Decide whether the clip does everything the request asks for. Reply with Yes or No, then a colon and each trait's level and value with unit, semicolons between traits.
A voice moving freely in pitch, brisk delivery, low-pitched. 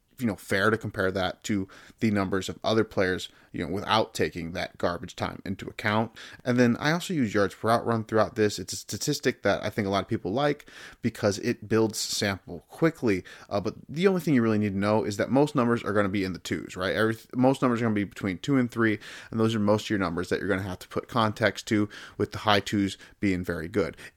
No: average, 3.2 semitones; fast, 260 wpm; low, 110 Hz